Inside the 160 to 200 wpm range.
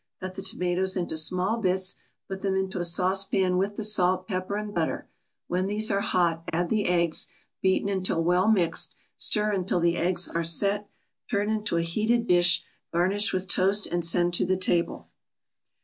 Yes: average, 180 wpm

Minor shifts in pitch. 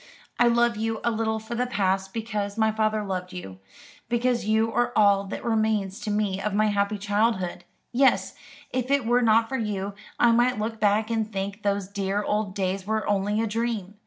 Yes: narrow, 2.2 semitones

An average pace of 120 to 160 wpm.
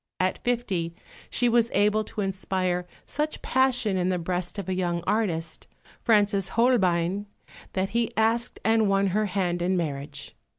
Yes: average, 155 wpm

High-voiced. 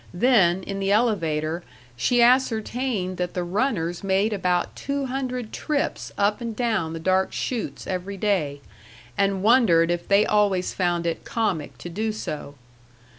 Yes: high, 195 Hz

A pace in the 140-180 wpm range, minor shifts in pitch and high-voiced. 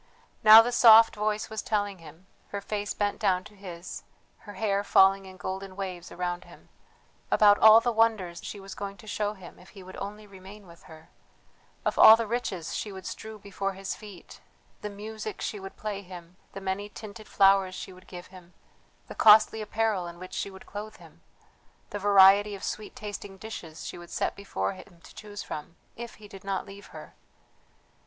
No: average, 195 wpm; narrow, 2.1 semitones; high, 200 Hz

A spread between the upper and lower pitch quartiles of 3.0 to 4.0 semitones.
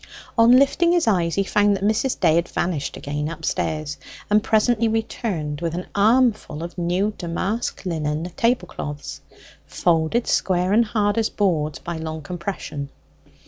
No: wide, 5.4 semitones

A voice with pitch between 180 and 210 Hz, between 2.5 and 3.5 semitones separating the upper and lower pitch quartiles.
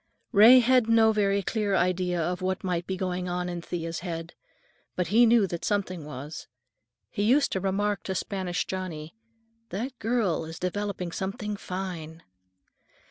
Yes: medium, 185 Hz; average, 3.0 semitones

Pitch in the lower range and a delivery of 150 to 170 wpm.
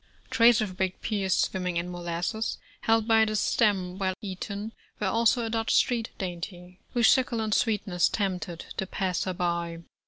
No: high, 195 Hz; average, 155 wpm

